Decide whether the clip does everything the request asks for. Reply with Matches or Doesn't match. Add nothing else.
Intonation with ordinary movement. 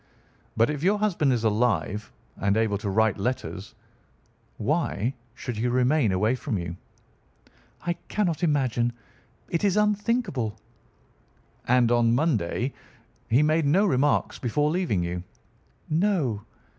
Doesn't match